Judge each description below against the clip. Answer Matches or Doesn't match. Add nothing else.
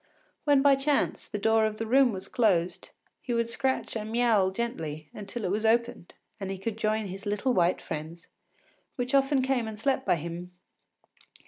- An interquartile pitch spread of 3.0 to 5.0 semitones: Matches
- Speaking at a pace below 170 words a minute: Doesn't match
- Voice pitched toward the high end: Matches